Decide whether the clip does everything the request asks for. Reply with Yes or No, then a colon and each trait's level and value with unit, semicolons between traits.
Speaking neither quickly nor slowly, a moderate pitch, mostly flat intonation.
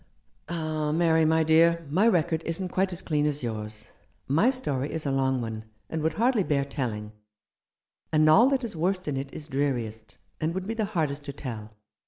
No: average, 195 wpm; medium, 155 Hz; average, 4.1 semitones